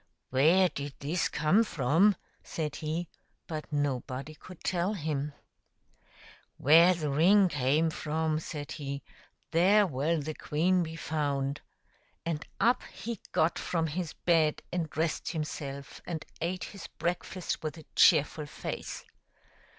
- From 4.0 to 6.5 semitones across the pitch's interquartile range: No, average, 3.0 semitones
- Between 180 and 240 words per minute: No, average, 145 wpm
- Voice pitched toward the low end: No, medium, 160 Hz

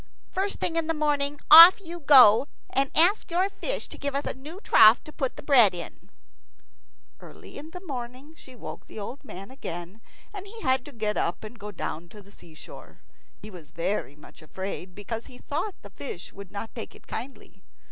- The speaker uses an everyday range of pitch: No, wide, 7.0 semitones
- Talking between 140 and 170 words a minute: No, average, 200 wpm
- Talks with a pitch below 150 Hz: No, very high, 260 Hz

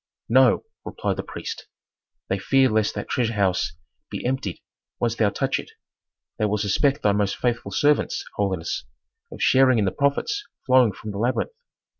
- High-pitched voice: No, low, 115 Hz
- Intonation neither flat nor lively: Yes, average, 4.3 semitones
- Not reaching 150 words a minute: No, average, 165 wpm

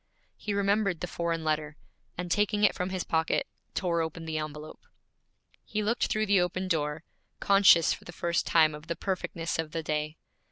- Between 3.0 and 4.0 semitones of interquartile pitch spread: Yes, average, 3.5 semitones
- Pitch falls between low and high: Yes, medium, 170 Hz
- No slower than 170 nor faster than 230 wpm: Yes, average, 185 wpm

